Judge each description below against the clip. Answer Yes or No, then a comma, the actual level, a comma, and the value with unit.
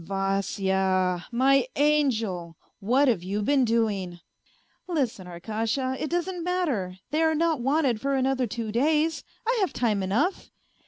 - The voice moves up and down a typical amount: No, wide, 7.3 semitones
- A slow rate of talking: No, average, 160 wpm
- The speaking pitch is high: Yes, high, 240 Hz